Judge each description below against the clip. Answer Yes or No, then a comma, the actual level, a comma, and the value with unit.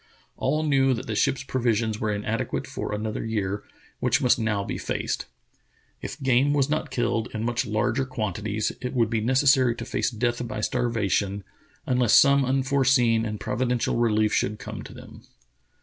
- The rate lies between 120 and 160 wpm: No, average, 170 wpm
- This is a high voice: No, low, 120 Hz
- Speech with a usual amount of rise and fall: Yes, average, 3.2 semitones